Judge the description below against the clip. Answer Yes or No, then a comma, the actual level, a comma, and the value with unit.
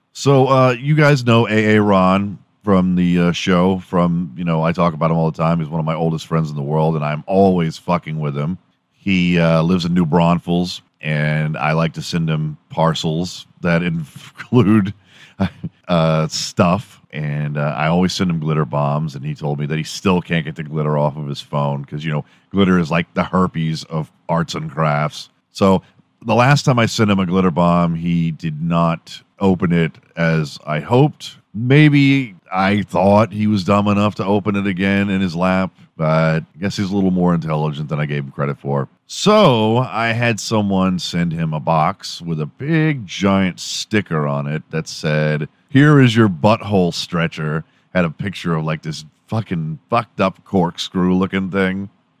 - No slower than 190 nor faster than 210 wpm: Yes, average, 195 wpm